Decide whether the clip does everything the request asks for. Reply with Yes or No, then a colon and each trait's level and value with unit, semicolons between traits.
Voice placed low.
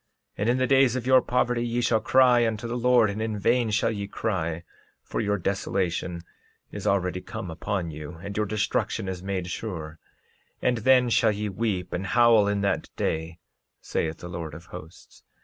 Yes: low, 105 Hz